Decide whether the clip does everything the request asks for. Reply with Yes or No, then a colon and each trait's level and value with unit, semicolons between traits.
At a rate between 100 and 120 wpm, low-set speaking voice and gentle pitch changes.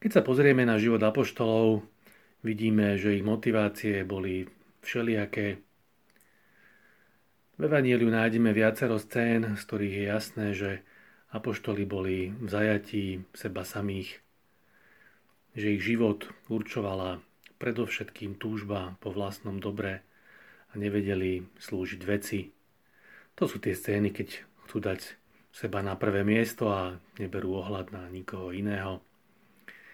Yes: average, 115 wpm; low, 105 Hz; narrow, 2.3 semitones